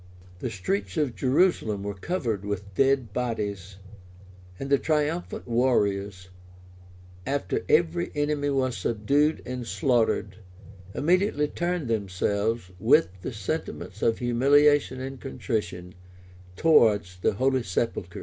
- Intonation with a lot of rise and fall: Yes, wide, 6.1 semitones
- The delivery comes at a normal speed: No, slow, 115 wpm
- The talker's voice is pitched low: Yes, low, 120 Hz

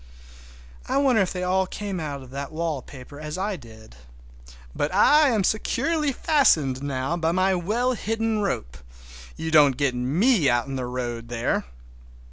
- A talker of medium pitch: Yes, medium, 155 Hz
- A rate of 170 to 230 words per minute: No, average, 155 wpm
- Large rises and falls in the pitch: Yes, wide, 8.3 semitones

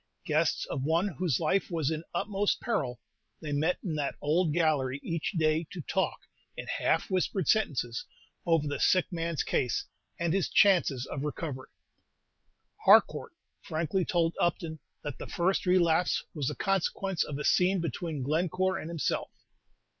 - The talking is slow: No, average, 155 wpm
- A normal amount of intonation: Yes, average, 3.6 semitones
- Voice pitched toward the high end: No, medium, 165 Hz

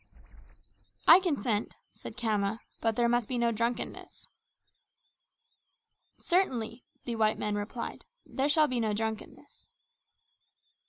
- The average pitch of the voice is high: Yes, high, 230 Hz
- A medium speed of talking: No, slow, 110 wpm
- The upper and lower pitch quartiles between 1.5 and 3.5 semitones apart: Yes, narrow, 2.4 semitones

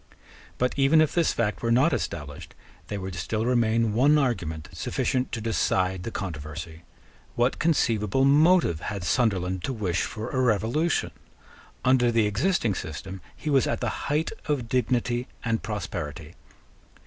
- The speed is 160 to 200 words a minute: No, average, 150 wpm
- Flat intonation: No, wide, 5.6 semitones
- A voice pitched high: No, low, 115 Hz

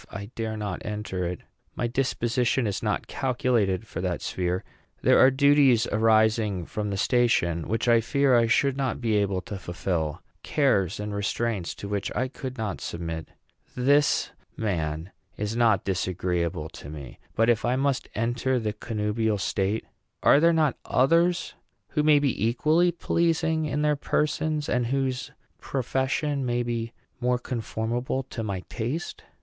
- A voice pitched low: Yes, low, 115 Hz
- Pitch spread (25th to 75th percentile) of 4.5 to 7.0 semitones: Yes, average, 4.9 semitones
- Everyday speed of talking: Yes, average, 155 wpm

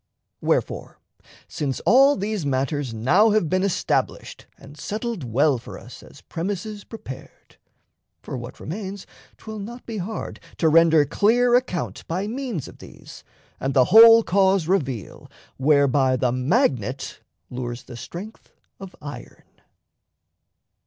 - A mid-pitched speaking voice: Yes, medium, 170 Hz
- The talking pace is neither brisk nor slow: No, slow, 130 wpm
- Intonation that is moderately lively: No, wide, 8.1 semitones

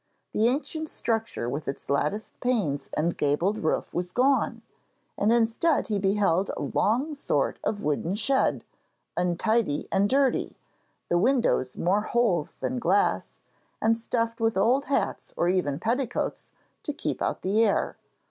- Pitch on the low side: No, high, 215 Hz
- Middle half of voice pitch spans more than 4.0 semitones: Yes, wide, 5.5 semitones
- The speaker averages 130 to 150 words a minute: Yes, average, 145 wpm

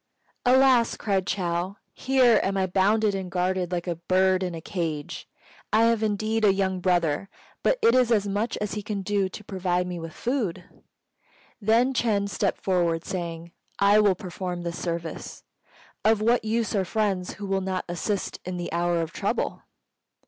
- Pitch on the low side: No, high, 190 Hz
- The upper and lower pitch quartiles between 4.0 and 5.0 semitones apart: No, average, 3.4 semitones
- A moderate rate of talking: Yes, average, 175 wpm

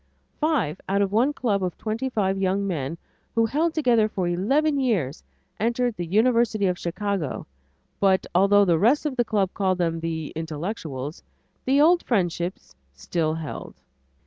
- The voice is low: No, high, 200 Hz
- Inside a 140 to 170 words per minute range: Yes, average, 160 wpm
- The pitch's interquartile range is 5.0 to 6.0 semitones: Yes, wide, 5.6 semitones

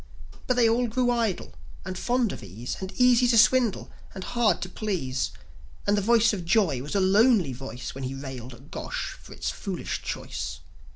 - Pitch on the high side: Yes, high, 195 Hz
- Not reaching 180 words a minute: No, average, 190 wpm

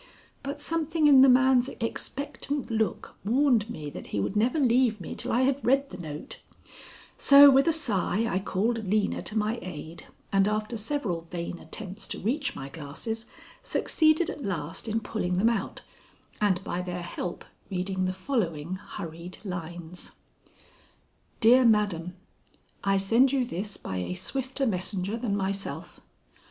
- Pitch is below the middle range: No, high, 210 Hz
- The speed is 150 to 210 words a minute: Yes, average, 155 wpm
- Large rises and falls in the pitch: Yes, wide, 6.0 semitones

